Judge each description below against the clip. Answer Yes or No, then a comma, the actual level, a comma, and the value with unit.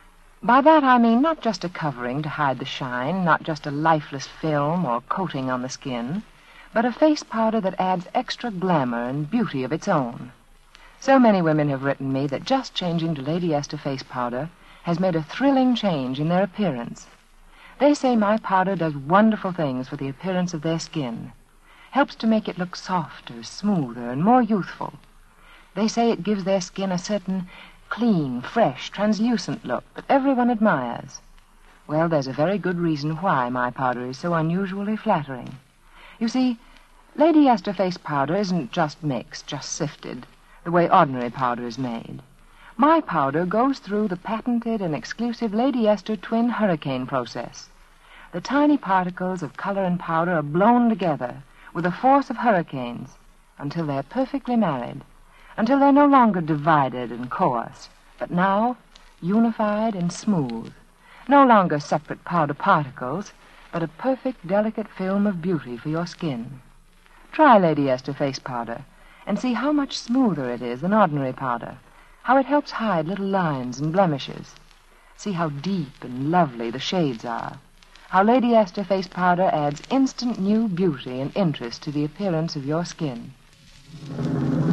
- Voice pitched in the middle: Yes, medium, 180 Hz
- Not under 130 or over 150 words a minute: No, average, 165 wpm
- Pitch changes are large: Yes, wide, 7.1 semitones